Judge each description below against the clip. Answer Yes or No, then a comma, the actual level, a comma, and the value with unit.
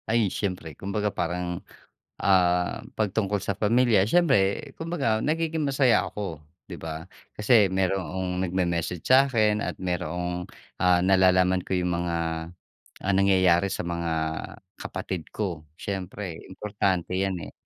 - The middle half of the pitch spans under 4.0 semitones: Yes, average, 3.0 semitones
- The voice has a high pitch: No, very low, 95 Hz